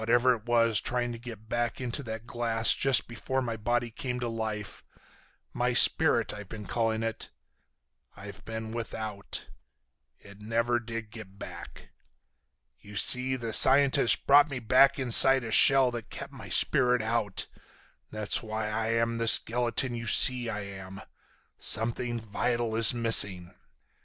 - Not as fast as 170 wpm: Yes, average, 140 wpm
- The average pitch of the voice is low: Yes, low, 115 Hz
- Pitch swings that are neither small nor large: No, narrow, 1.8 semitones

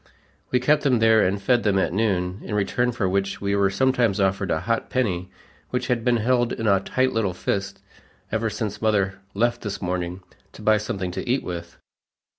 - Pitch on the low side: Yes, low, 105 Hz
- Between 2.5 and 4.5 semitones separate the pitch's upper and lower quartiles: Yes, average, 3.7 semitones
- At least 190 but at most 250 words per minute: Yes, average, 200 wpm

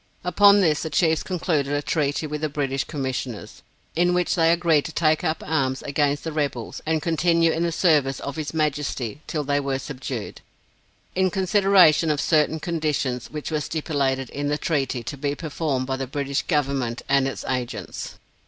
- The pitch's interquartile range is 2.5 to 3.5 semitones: Yes, average, 2.9 semitones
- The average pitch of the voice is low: No, medium, 150 Hz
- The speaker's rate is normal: Yes, average, 180 wpm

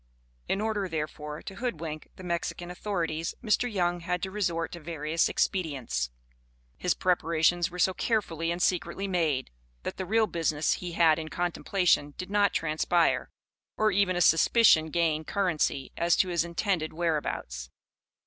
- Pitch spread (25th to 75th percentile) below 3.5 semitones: Yes, average, 2.9 semitones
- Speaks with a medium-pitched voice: Yes, medium, 170 Hz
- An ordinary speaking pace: Yes, average, 150 wpm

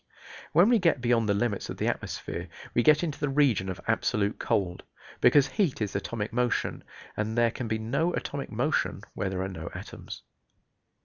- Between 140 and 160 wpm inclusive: No, average, 185 wpm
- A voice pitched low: Yes, low, 120 Hz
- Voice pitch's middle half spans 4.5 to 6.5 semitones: Yes, wide, 5.6 semitones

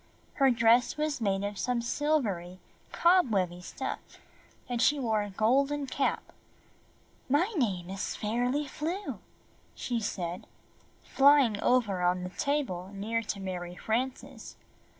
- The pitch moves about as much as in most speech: No, wide, 6.2 semitones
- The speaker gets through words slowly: Yes, slow, 125 wpm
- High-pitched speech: Yes, high, 230 Hz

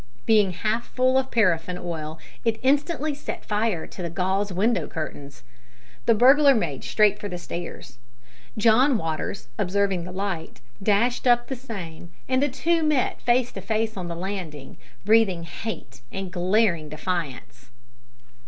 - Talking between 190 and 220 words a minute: No, average, 150 wpm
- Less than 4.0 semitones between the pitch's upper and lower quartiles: No, wide, 5.5 semitones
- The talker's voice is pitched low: No, high, 200 Hz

